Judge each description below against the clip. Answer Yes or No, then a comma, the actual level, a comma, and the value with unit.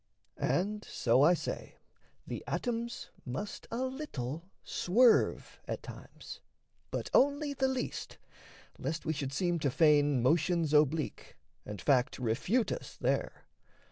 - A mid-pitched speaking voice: Yes, medium, 165 Hz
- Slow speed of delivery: Yes, slow, 125 wpm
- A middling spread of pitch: No, wide, 8.9 semitones